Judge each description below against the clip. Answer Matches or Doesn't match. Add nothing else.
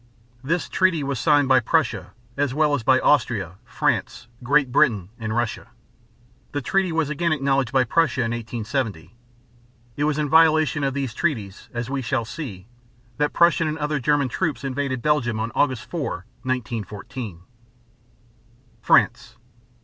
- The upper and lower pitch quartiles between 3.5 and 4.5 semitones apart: Matches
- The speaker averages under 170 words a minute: Matches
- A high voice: Doesn't match